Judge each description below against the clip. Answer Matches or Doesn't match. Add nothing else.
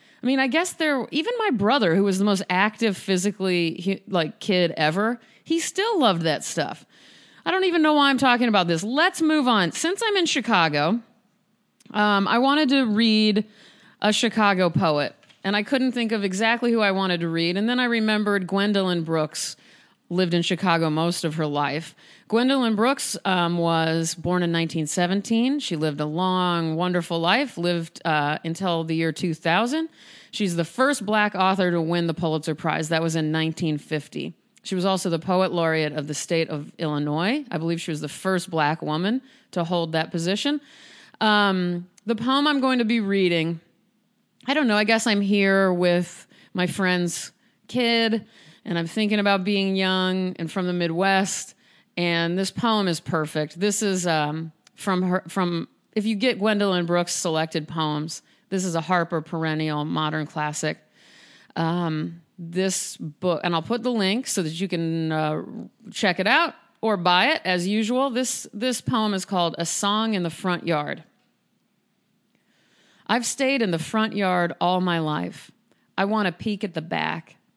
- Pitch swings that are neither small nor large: Matches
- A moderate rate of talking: Matches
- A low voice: Doesn't match